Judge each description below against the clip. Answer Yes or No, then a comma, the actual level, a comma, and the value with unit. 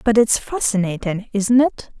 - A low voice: No, high, 220 Hz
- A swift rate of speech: No, average, 150 wpm